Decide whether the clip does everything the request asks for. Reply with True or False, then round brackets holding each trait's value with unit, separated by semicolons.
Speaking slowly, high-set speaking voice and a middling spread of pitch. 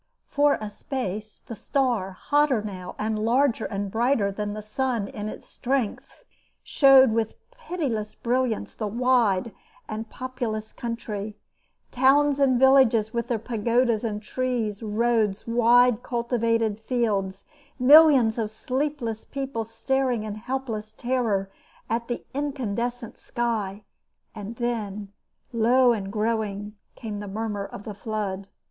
True (125 wpm; 230 Hz; 3.1 semitones)